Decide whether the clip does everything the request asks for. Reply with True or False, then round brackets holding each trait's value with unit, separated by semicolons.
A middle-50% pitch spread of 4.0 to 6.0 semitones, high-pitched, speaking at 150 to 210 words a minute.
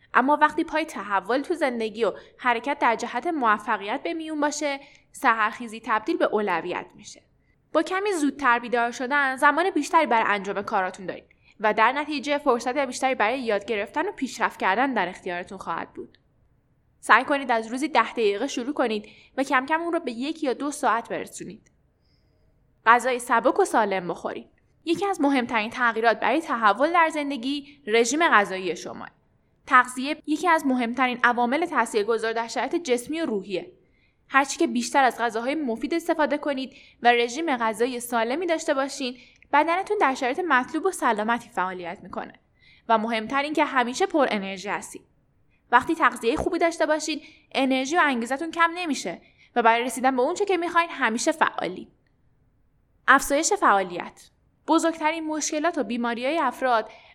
True (5.0 semitones; 260 Hz; 155 wpm)